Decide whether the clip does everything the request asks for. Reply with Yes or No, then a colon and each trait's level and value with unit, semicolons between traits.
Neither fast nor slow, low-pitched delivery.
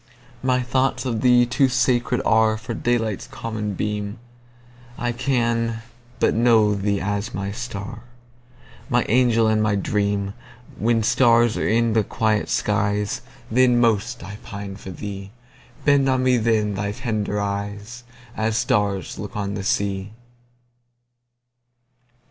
No: slow, 115 wpm; low, 115 Hz